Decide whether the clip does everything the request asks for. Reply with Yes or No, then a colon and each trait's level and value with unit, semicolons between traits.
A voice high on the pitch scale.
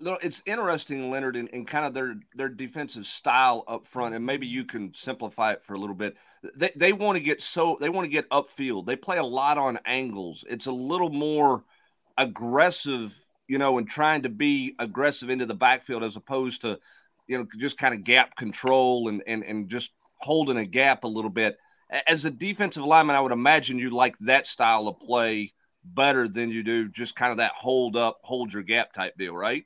No: low, 130 Hz